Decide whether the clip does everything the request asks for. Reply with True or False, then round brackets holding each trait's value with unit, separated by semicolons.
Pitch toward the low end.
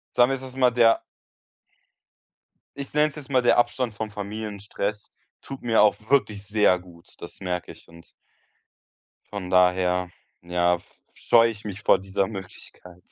True (105 Hz)